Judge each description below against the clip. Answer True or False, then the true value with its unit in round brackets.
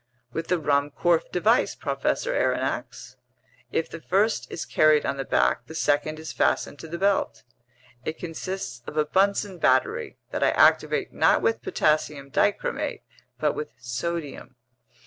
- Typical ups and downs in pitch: True (3.8 semitones)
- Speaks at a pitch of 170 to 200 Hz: False (155 Hz)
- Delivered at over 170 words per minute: False (145 wpm)